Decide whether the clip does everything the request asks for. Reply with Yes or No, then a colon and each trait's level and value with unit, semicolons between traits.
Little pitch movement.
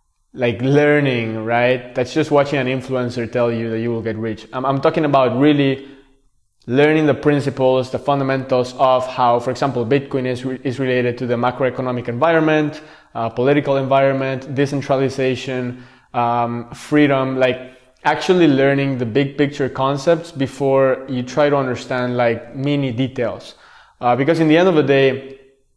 Yes: narrow, 2.1 semitones